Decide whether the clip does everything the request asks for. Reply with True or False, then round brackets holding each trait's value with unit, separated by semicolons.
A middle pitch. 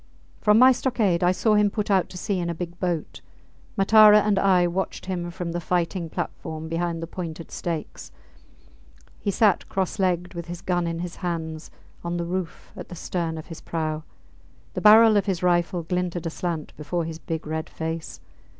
True (175 Hz)